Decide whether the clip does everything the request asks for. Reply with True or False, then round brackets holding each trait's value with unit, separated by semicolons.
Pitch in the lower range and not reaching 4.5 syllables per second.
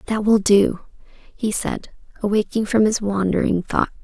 False (205 Hz; 4.3 syllables/s)